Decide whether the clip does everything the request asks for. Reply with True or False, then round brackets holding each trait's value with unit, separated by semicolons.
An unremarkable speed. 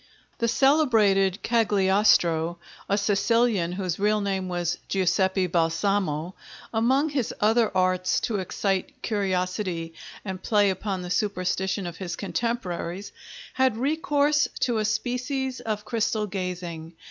False (120 wpm)